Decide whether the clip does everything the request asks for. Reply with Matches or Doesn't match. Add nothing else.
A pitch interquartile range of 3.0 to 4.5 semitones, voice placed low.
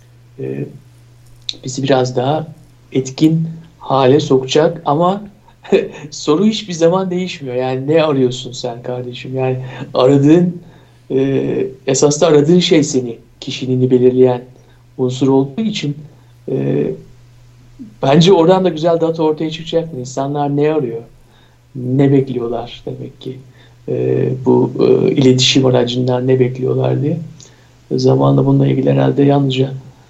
Matches